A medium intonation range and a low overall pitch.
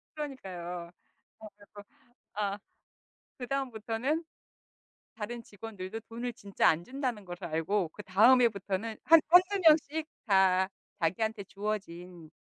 No: average, 4.9 semitones; high, 210 Hz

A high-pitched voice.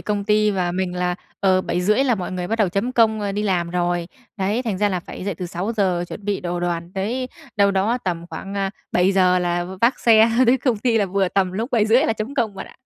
Yes: high, 195 Hz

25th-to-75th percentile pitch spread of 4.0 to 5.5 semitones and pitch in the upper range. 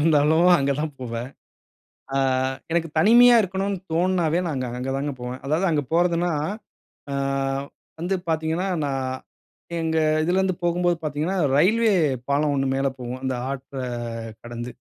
No: average, 4.5 semitones; medium, 160 Hz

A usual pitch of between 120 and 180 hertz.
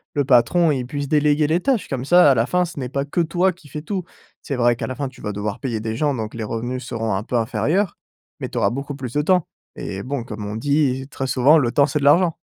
Yes: medium, 140 Hz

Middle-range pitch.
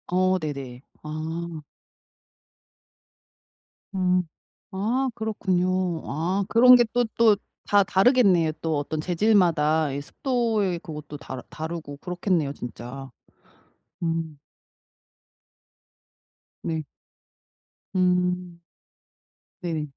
Yes: medium, 175 Hz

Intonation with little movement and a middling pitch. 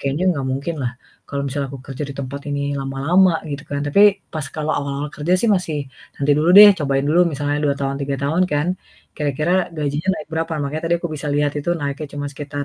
Yes: narrow, 1.8 semitones; medium, 145 Hz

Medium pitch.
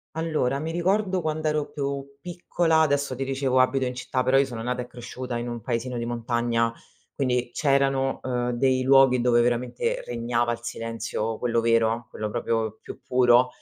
No: low, 125 Hz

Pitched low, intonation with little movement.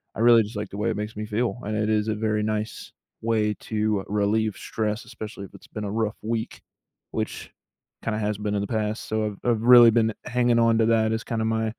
Yes: low, 110 Hz; narrow, 1.2 semitones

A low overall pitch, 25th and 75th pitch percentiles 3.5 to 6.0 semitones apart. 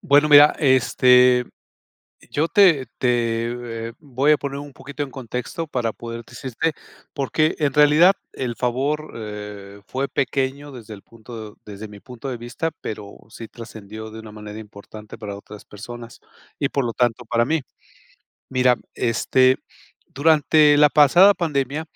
Yes: low, 125 Hz; average, 4.2 semitones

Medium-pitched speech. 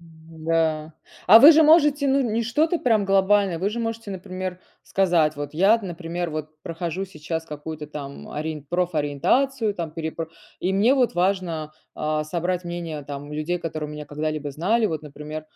Yes: medium, 170 Hz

